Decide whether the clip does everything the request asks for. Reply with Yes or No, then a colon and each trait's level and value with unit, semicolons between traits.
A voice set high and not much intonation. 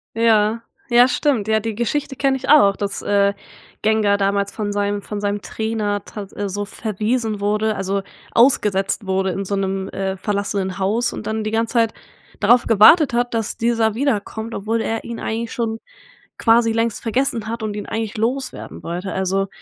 Yes: high, 220 Hz; narrow, 2.3 semitones